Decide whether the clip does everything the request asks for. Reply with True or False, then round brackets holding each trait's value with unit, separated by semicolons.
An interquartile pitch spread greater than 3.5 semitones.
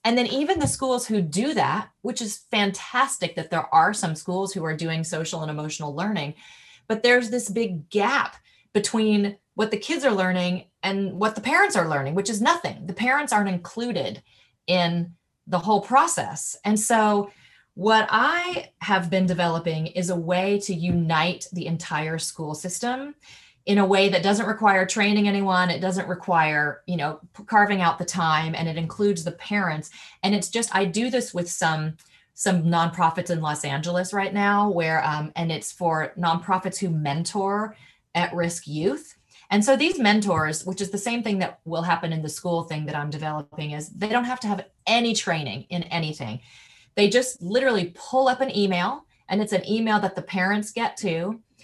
True (4.1 semitones)